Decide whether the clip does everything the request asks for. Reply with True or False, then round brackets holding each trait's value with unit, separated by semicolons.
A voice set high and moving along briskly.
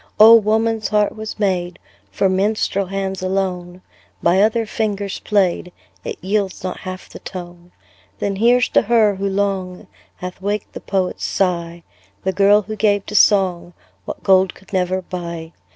False (195 Hz; 155 wpm)